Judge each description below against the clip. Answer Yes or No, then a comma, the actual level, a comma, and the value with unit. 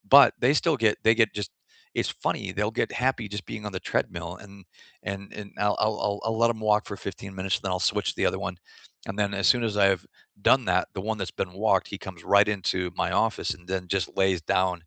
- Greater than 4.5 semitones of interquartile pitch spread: No, narrow, 2.4 semitones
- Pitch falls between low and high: No, low, 100 Hz